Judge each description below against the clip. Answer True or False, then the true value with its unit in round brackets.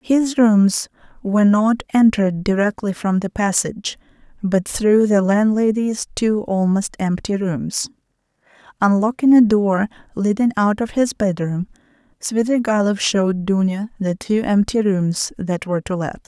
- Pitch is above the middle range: True (205 Hz)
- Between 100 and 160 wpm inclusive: True (135 wpm)